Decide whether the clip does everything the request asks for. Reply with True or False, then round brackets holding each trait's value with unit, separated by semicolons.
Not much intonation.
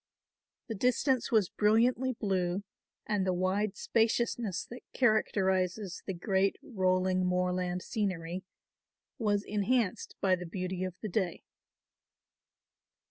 False (3.1 semitones)